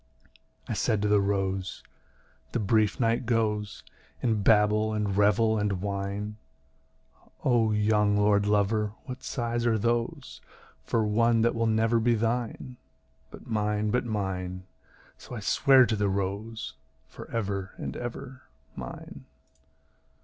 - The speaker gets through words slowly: Yes, slow, 130 wpm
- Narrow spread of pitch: Yes, narrow, 2.1 semitones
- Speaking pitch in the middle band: No, low, 105 Hz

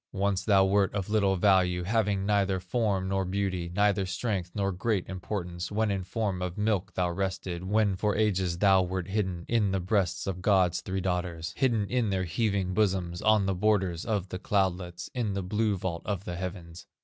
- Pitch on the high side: No, very low, 95 Hz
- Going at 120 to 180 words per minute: No, average, 190 wpm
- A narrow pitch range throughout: Yes, narrow, 2.3 semitones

